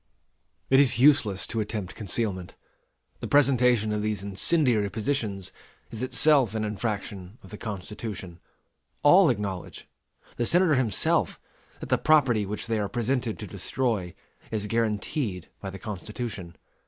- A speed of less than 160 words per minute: Yes, slow, 135 wpm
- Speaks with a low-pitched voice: Yes, low, 110 Hz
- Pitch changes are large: No, average, 3.8 semitones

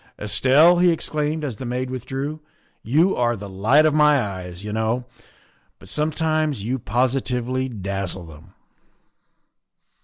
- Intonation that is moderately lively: No, wide, 6.2 semitones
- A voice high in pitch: No, low, 130 Hz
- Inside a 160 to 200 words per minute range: No, average, 145 wpm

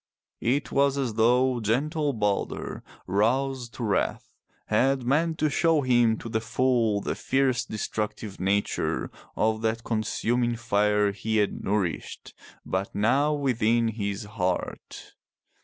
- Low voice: Yes, low, 115 Hz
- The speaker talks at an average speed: No, slow, 130 wpm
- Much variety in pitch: No, average, 3.8 semitones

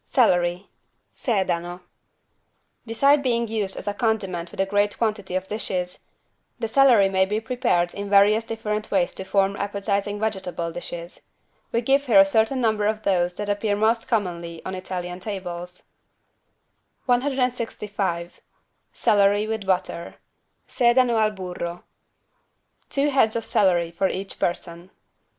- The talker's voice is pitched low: No, high, 205 Hz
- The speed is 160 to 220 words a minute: No, slow, 135 wpm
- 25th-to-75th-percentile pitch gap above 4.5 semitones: No, average, 3.6 semitones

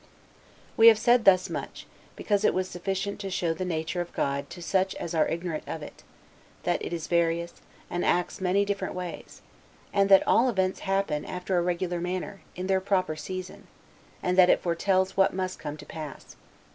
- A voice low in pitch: No, medium, 185 Hz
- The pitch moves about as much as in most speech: No, narrow, 2.1 semitones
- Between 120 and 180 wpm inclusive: No, average, 195 wpm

